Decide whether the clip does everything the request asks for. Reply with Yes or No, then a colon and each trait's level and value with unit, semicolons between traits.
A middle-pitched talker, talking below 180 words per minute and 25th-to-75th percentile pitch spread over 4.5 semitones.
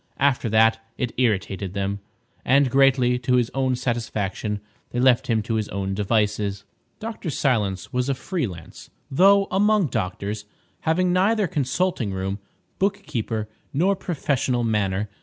No: low, 120 Hz; average, 140 wpm; wide, 5.4 semitones